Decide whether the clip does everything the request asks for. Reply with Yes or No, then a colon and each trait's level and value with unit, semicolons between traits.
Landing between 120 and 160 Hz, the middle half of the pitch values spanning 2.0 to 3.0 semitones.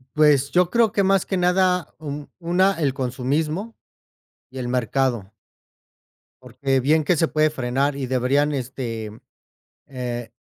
No: medium, 140 Hz; average, 5.1 semitones